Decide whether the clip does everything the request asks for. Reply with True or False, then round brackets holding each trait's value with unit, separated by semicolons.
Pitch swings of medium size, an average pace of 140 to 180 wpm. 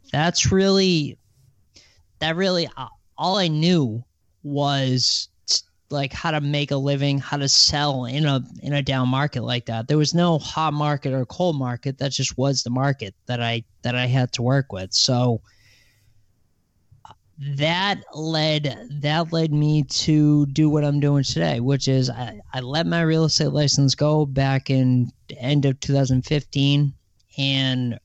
True (3.3 semitones; 165 wpm)